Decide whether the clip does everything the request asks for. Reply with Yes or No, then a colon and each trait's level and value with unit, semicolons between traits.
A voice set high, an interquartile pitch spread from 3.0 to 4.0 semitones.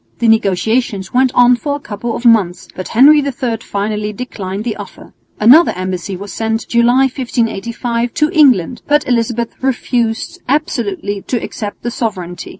Yes: high, 230 Hz; average, 3.5 semitones